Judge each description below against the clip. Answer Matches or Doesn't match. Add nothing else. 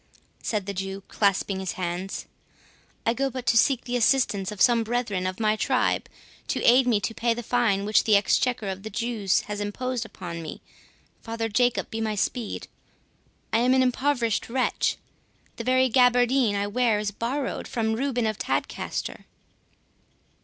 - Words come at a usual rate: Matches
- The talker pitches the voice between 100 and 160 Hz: Doesn't match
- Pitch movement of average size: Matches